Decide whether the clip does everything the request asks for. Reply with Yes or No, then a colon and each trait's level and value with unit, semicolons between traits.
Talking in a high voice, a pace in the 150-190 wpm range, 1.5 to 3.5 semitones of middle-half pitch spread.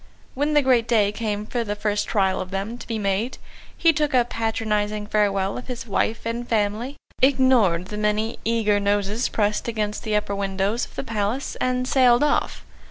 Yes: high, 215 Hz; average, 185 wpm; average, 2.9 semitones